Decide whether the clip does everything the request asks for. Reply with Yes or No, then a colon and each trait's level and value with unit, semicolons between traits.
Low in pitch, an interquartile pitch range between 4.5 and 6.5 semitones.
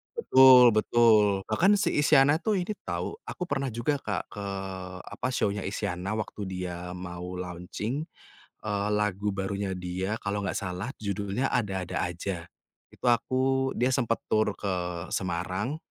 Yes: low, 105 Hz; average, 5.1 semitones